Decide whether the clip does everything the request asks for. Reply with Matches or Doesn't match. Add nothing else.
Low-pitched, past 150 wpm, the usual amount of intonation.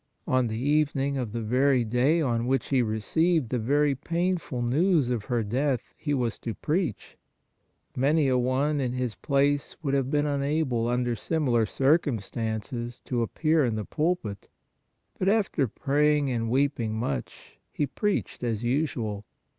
Matches